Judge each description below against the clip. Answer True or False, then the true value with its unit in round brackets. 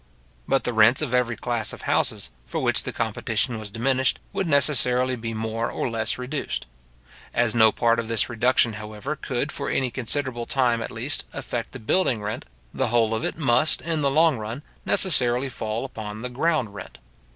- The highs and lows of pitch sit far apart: False (3.0 semitones)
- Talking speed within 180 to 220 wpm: True (185 wpm)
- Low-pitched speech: True (120 Hz)